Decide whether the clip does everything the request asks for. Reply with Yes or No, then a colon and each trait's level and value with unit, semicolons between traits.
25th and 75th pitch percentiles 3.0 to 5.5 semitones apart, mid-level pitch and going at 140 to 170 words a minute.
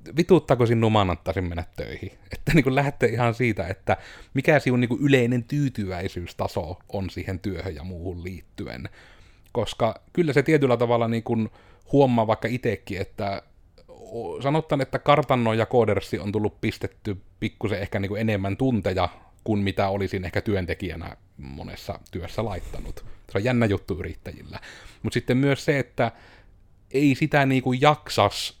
No: average, 4.8 semitones; low, 110 Hz; average, 145 wpm